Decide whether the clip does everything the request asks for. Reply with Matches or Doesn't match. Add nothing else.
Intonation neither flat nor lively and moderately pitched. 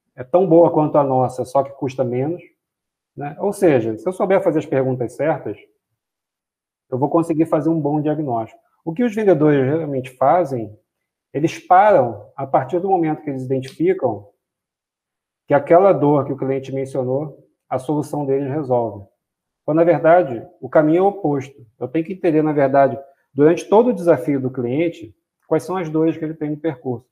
Matches